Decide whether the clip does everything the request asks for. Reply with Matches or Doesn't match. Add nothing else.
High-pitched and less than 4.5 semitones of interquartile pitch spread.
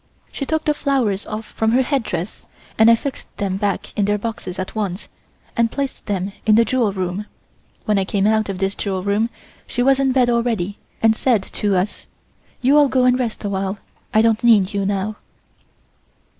Matches